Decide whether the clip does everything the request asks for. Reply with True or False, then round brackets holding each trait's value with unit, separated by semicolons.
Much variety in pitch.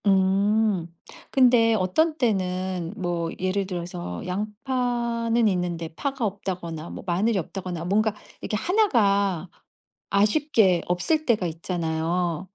False (4.3 semitones)